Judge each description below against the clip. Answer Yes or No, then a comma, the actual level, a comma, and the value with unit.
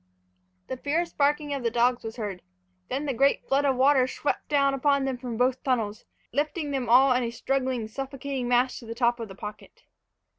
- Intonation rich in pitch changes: No, average, 2.7 semitones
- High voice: Yes, very high, 260 Hz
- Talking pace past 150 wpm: Yes, average, 200 wpm